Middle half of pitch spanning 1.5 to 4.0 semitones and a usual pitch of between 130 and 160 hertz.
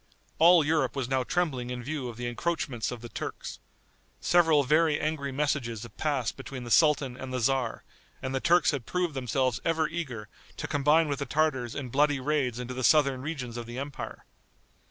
Yes: average, 3.6 semitones; low, 135 Hz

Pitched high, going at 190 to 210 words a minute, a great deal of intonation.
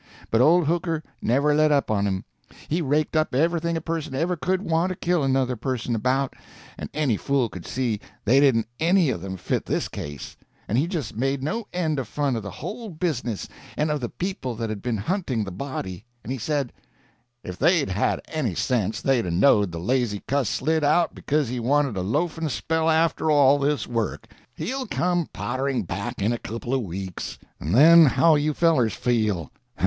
No: low, 135 Hz; average, 195 wpm; wide, 5.9 semitones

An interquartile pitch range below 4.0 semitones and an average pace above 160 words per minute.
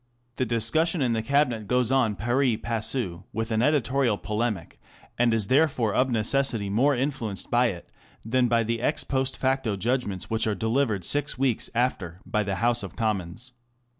Yes: average, 3.5 semitones; average, 170 wpm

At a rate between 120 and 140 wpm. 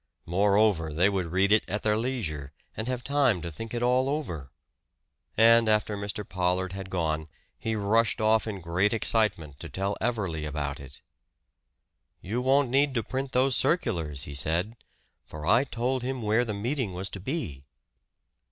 No: average, 170 wpm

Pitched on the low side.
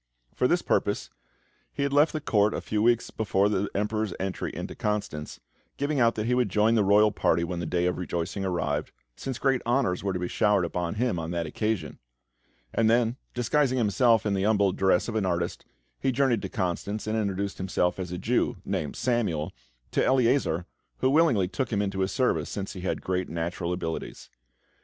Yes: low, 100 Hz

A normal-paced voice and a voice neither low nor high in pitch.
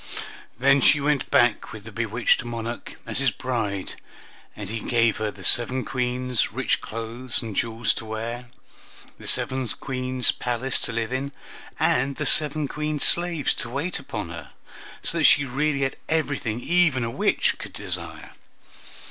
No: average, 160 wpm; low, 125 Hz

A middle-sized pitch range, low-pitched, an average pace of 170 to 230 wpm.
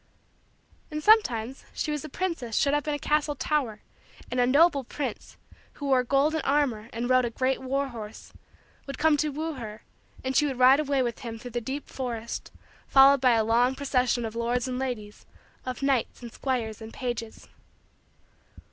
No: average, 3.1 semitones; very high, 255 Hz; average, 185 wpm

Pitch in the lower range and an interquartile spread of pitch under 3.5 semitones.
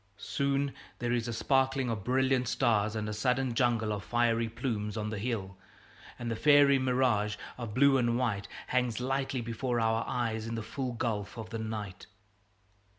Yes: low, 120 Hz; average, 2.9 semitones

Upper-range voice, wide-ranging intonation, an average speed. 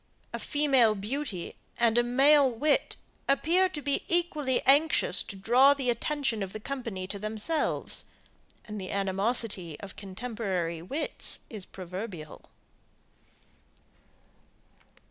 No: high, 235 Hz; wide, 6.2 semitones; slow, 115 wpm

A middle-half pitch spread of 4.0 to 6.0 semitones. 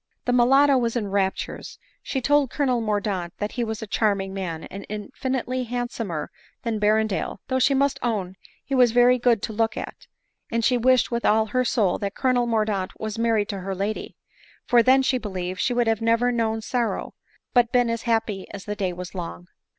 No: average, 3.4 semitones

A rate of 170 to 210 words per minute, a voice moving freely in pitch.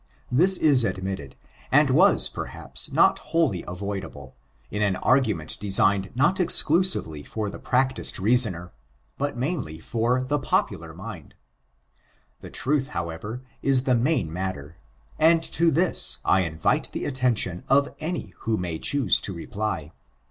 No: slow, 135 wpm; wide, 7.2 semitones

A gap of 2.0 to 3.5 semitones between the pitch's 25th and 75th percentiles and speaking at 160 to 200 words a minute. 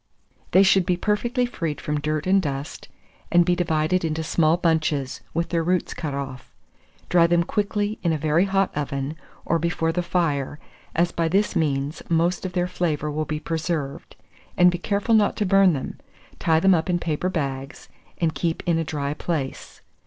Yes: average, 3.0 semitones; average, 185 wpm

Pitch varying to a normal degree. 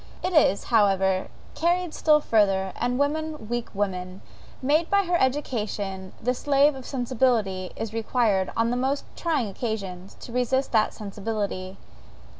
No: wide, 5.8 semitones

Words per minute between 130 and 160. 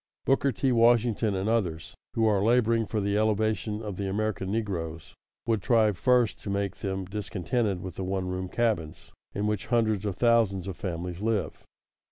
No: average, 175 wpm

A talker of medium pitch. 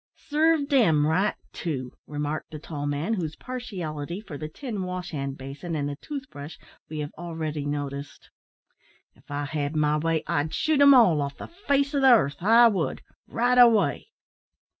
Yes: medium, 160 Hz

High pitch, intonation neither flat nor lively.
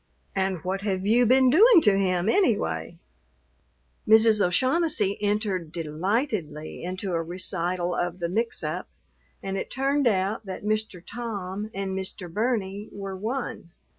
Yes: high, 195 Hz; average, 3.6 semitones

